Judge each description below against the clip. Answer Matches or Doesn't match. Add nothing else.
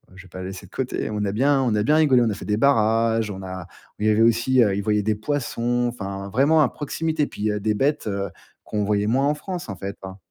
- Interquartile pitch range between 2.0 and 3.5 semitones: Doesn't match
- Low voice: Matches